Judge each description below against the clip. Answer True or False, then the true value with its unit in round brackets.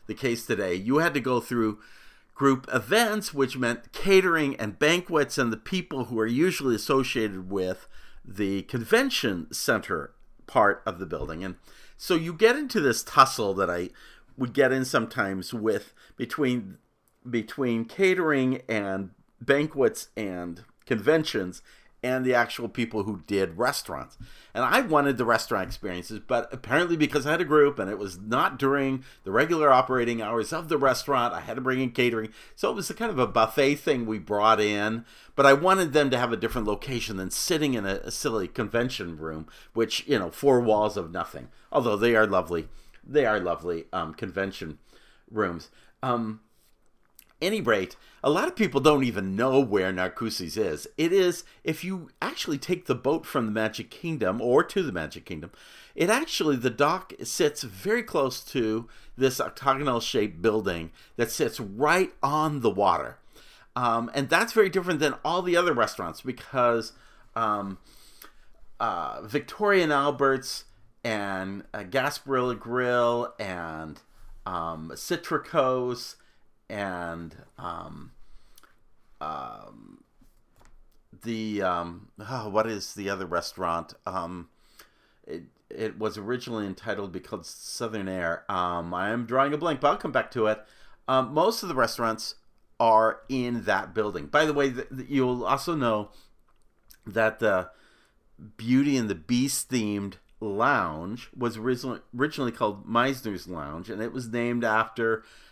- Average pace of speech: True (155 wpm)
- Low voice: True (120 Hz)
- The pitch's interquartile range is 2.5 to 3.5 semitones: False (4.7 semitones)